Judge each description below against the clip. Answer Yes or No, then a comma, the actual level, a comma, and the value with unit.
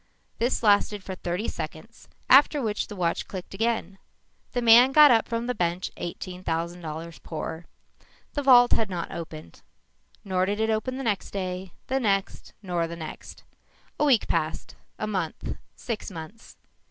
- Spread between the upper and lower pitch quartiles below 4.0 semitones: No, average, 5.0 semitones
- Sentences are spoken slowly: No, average, 165 wpm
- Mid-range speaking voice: No, high, 195 Hz